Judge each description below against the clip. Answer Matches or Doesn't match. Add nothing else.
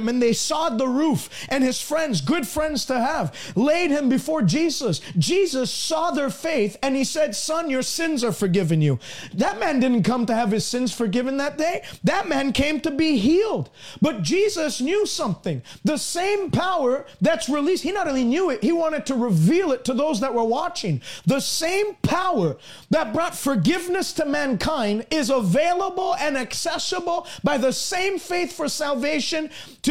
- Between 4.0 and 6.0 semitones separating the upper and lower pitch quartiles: Matches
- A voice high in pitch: Matches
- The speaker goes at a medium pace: Matches